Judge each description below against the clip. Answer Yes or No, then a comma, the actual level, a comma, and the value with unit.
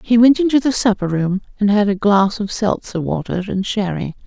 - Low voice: No, high, 205 Hz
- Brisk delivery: Yes, fast, 210 wpm